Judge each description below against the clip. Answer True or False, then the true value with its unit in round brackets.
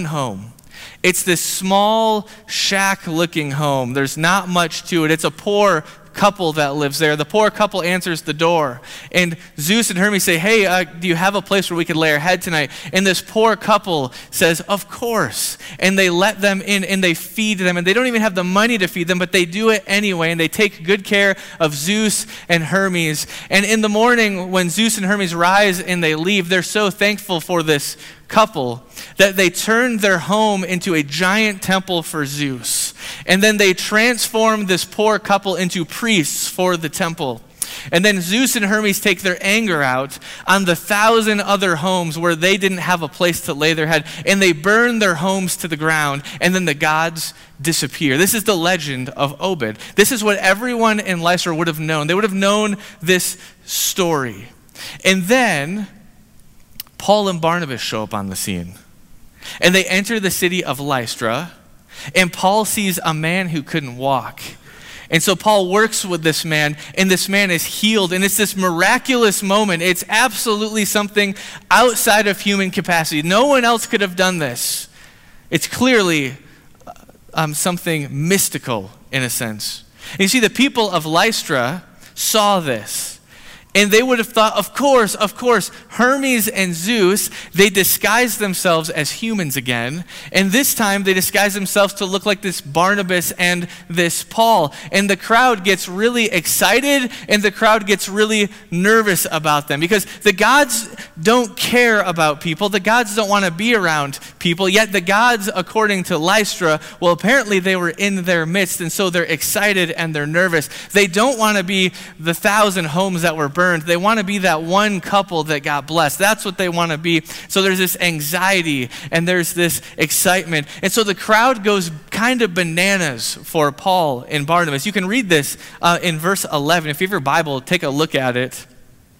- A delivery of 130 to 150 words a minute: False (185 wpm)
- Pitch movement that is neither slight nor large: True (4.0 semitones)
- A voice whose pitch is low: False (185 Hz)